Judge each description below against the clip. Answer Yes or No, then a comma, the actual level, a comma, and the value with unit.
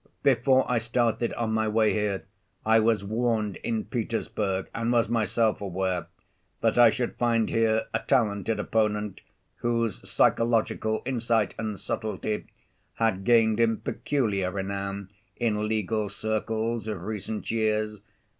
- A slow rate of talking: Yes, slow, 130 wpm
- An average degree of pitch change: No, narrow, 1.7 semitones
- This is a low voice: Yes, low, 110 Hz